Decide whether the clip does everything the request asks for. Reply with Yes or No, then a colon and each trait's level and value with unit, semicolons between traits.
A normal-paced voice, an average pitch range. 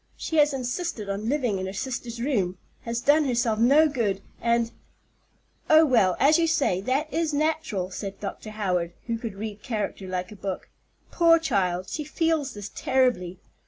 No: average, 170 wpm; wide, 6.9 semitones